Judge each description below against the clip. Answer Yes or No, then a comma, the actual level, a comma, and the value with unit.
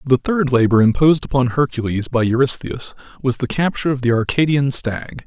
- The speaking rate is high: No, average, 170 wpm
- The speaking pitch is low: Yes, low, 130 Hz